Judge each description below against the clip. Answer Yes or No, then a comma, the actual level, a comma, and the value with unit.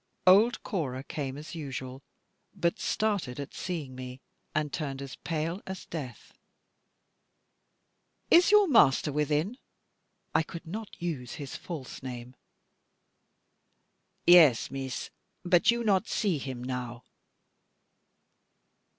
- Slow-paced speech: Yes, slow, 110 wpm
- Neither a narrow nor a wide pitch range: No, wide, 5.7 semitones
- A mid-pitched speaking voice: Yes, medium, 150 Hz